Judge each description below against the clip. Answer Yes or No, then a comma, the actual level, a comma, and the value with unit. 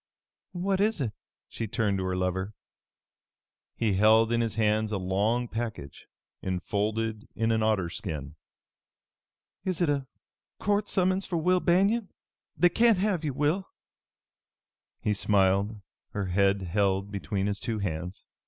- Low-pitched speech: Yes, low, 110 Hz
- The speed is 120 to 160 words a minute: Yes, average, 140 wpm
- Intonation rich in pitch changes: Yes, wide, 8.3 semitones